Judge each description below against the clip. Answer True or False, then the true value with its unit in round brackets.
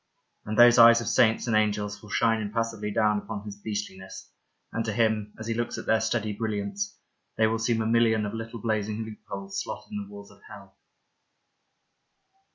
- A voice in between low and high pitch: False (110 Hz)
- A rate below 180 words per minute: False (185 wpm)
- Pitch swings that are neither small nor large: False (1.7 semitones)